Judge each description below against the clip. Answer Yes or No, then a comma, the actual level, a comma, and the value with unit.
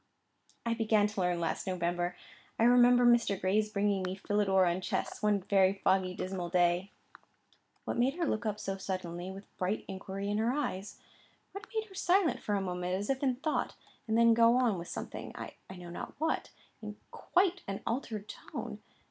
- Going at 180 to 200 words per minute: Yes, average, 185 wpm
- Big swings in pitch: No, average, 4.0 semitones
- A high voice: Yes, high, 205 Hz